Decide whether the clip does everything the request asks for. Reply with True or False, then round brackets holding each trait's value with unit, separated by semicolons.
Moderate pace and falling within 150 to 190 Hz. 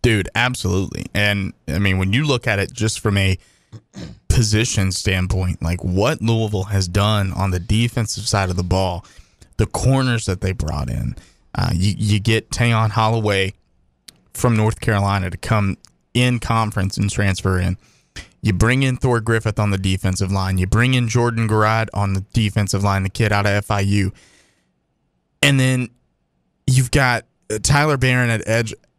False (165 wpm; 105 Hz)